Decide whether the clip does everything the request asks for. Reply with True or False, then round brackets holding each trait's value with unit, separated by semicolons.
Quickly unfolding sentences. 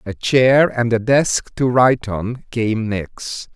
False (170 wpm)